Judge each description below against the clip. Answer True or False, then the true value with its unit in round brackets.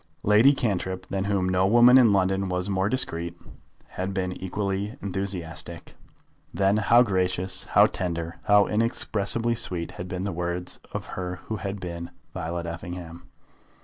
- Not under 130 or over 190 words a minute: True (150 wpm)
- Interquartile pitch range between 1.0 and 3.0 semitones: True (2.4 semitones)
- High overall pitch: False (95 Hz)